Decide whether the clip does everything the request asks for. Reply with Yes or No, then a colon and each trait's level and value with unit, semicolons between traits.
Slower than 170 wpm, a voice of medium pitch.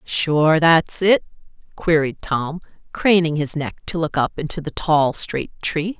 Yes: average, 160 wpm; medium, 160 Hz